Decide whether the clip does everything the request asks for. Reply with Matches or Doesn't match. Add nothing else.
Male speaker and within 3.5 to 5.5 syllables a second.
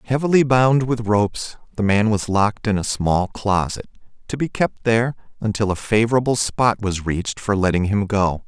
Matches